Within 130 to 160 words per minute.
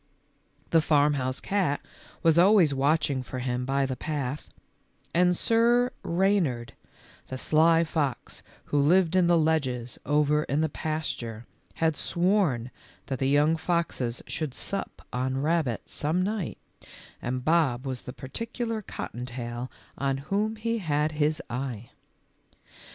Yes: slow, 135 wpm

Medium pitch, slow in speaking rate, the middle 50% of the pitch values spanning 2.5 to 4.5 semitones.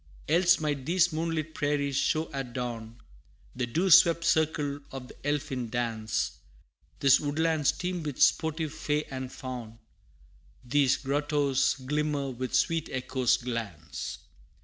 Yes: medium, 145 Hz; slow, 125 wpm; average, 3.7 semitones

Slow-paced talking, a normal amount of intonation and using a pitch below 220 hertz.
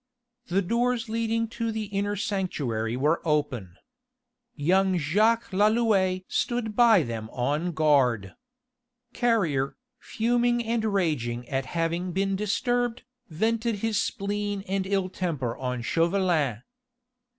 No: slow, 115 wpm; wide, 7.0 semitones; high, 190 Hz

